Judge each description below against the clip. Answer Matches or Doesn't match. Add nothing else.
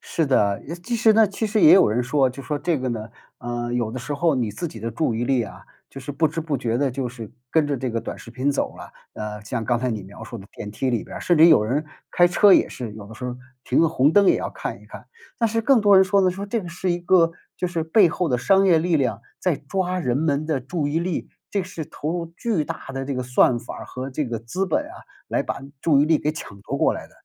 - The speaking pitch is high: Doesn't match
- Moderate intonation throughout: Doesn't match